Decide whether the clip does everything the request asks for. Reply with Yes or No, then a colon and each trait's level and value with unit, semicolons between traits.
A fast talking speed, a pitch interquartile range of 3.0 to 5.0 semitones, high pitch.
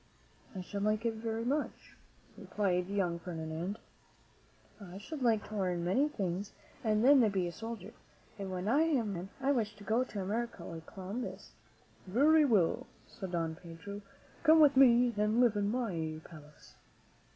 No: average, 170 wpm; average, 4.7 semitones; high, 205 Hz